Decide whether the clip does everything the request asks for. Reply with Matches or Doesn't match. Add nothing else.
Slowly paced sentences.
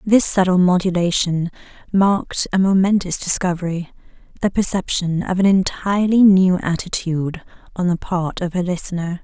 Matches